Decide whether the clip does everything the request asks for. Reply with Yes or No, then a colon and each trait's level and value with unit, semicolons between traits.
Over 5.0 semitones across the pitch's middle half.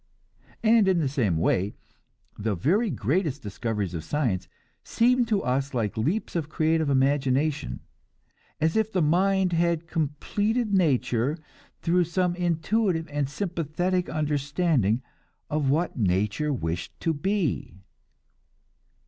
Yes: wide, 5.6 semitones